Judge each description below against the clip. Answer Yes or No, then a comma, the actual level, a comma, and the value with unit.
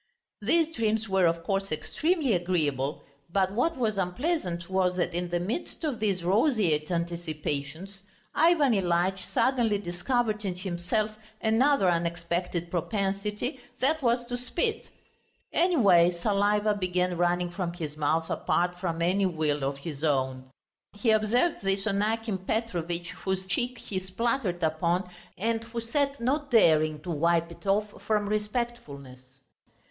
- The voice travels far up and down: No, average, 4.9 semitones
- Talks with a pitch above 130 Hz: Yes, high, 190 Hz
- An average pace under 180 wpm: Yes, average, 140 wpm